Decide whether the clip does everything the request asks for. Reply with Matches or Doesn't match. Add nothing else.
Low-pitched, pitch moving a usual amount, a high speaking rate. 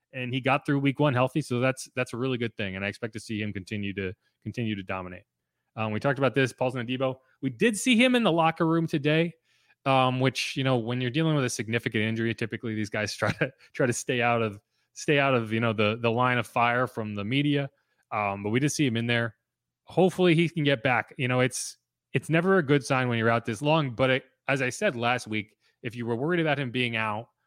Matches